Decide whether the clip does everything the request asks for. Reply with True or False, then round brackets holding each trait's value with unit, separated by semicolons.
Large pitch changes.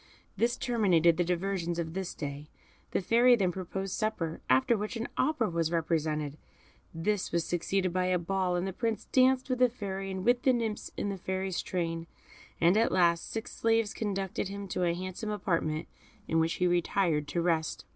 False (4.0 semitones)